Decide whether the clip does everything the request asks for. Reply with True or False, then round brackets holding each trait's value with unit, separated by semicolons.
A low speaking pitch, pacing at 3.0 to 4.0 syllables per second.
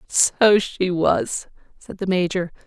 False (185 Hz; 3.8 syllables/s)